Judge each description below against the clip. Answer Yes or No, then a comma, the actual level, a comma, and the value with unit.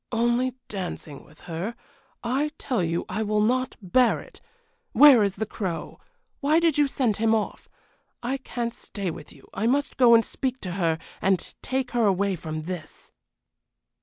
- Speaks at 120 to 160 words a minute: No, average, 170 wpm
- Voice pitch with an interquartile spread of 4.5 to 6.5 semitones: Yes, wide, 5.6 semitones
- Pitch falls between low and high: No, high, 220 Hz